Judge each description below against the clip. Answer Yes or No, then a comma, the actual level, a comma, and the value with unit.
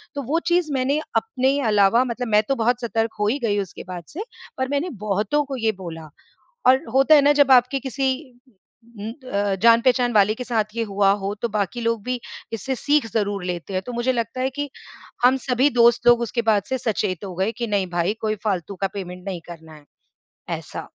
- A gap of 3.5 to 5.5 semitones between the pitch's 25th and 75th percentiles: Yes, average, 4.6 semitones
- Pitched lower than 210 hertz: No, high, 230 Hz